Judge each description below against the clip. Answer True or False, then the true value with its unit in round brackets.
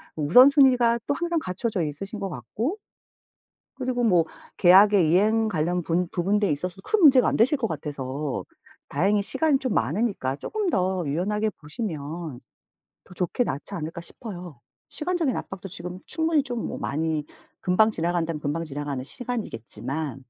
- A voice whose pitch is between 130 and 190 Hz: True (185 Hz)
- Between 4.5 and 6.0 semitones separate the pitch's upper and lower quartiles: False (7.0 semitones)